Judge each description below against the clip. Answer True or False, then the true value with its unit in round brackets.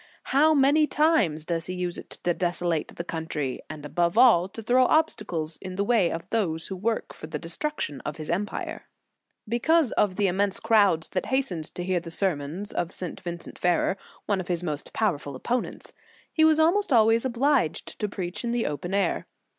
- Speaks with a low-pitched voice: False (185 Hz)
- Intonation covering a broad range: True (5.8 semitones)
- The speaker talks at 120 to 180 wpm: False (195 wpm)